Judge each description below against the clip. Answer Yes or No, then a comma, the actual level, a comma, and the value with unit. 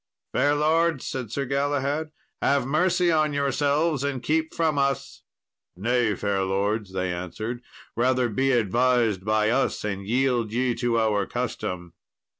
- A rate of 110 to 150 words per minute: Yes, average, 140 wpm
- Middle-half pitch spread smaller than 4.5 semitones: No, average, 5.0 semitones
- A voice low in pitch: Yes, low, 125 Hz